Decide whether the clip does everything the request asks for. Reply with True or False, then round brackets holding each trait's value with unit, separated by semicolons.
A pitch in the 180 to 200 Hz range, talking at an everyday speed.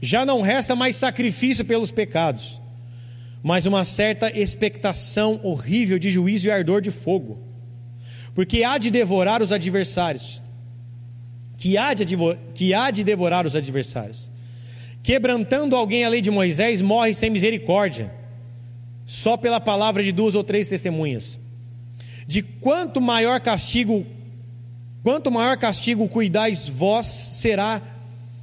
True (190 Hz; 130 wpm)